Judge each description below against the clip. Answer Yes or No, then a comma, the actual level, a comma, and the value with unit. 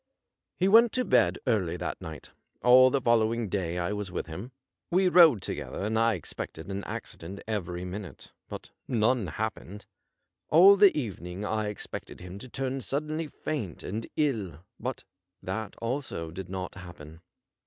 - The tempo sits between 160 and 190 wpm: Yes, average, 165 wpm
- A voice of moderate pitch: No, low, 105 Hz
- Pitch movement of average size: No, wide, 6.1 semitones